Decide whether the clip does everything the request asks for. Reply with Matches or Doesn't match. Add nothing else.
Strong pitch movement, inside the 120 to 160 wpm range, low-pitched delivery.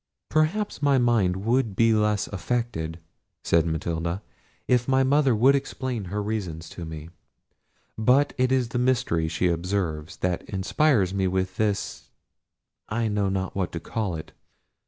Matches